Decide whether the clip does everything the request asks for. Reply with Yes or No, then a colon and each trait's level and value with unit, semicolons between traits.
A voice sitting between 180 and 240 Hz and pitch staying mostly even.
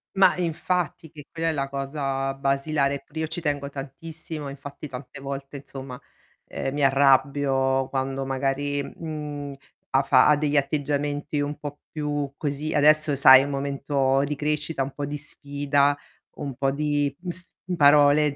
No: medium, 145 Hz; narrow, 1.5 semitones